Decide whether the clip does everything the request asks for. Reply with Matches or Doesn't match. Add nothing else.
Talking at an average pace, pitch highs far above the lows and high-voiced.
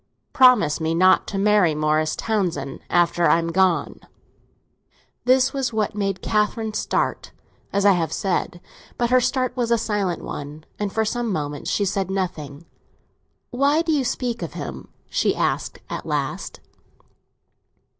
Matches